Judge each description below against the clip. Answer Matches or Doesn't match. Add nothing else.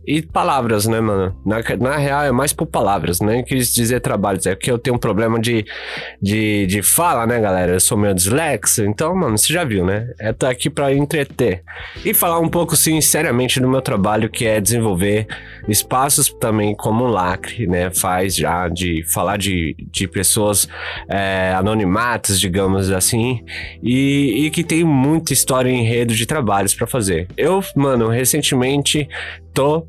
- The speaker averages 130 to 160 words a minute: Doesn't match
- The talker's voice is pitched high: Doesn't match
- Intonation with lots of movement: Matches